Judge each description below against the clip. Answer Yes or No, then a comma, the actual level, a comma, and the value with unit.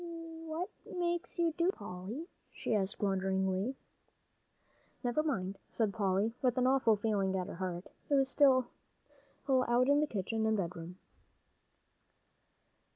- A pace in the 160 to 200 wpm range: No, average, 140 wpm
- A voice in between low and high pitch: No, high, 225 Hz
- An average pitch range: No, wide, 6.0 semitones